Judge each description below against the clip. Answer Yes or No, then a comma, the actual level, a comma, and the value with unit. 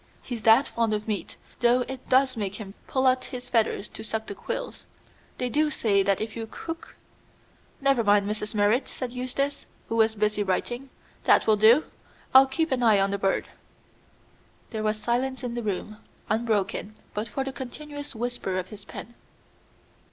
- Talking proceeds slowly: No, average, 180 wpm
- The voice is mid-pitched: No, high, 230 Hz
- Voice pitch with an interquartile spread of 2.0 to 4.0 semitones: Yes, average, 3.6 semitones